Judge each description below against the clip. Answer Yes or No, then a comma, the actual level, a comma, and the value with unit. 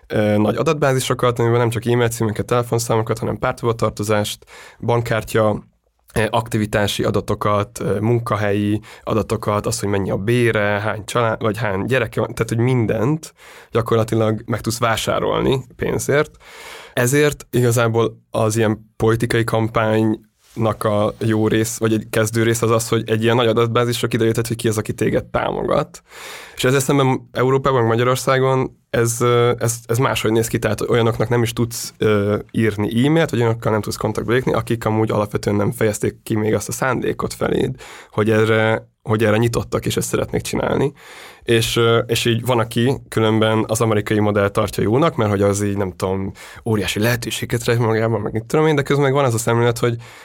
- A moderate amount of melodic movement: No, narrow, 1.8 semitones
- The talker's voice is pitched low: Yes, low, 115 Hz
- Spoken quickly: Yes, fast, 165 wpm